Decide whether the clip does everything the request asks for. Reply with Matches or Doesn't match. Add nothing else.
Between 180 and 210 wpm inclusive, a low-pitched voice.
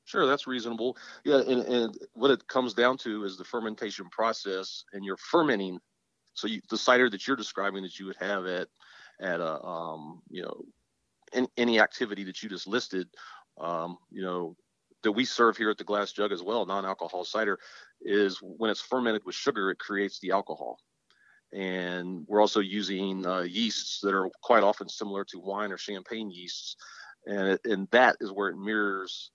Matches